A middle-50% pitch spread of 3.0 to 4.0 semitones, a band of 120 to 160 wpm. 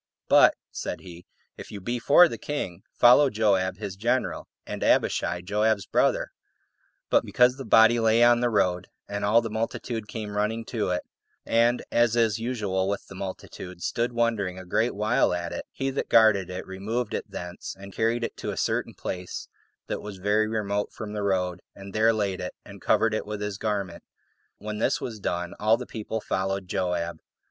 No: average, 3.3 semitones; average, 190 wpm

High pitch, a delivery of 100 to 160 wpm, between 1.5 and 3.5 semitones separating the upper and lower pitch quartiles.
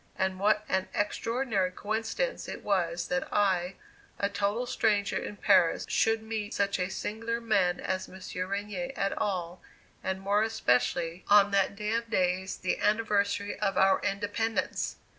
Yes: high, 200 Hz; average, 150 wpm; narrow, 2.5 semitones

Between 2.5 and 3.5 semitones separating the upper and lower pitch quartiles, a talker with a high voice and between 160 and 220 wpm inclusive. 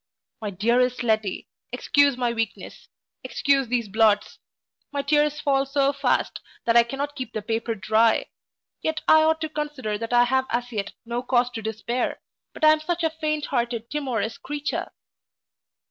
No: average, 4.2 semitones; very high, 250 Hz; average, 165 wpm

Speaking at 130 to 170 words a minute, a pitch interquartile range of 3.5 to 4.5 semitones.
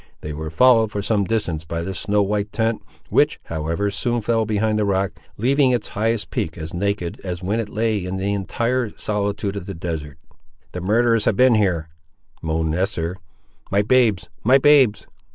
No: average, 180 wpm; average, 4.1 semitones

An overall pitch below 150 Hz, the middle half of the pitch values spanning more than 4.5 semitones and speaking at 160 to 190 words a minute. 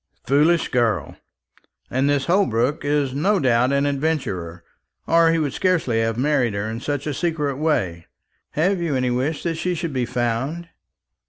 Yes: medium, 140 Hz; average, 5.0 semitones; average, 165 wpm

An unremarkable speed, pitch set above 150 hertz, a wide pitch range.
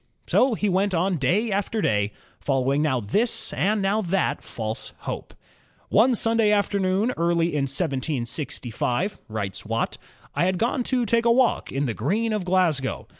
Yes: average, 160 wpm; medium, 185 Hz; wide, 7.7 semitones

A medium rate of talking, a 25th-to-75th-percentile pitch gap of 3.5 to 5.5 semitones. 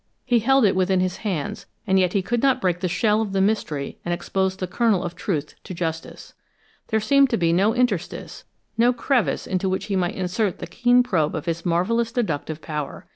No: fast, 210 wpm; average, 4.5 semitones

